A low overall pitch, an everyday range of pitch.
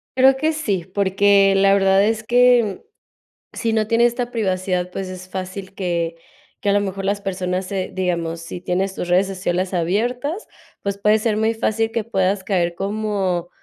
No: high, 195 Hz; average, 3.0 semitones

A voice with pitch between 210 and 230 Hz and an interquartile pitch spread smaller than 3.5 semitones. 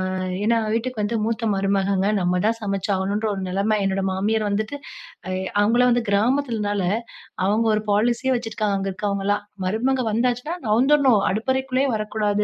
Yes: high, 215 Hz; average, 3.1 semitones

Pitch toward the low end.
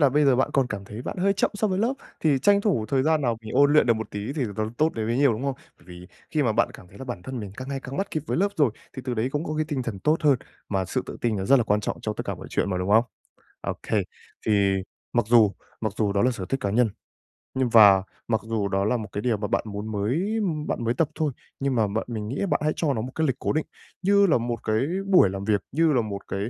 Yes: low, 120 Hz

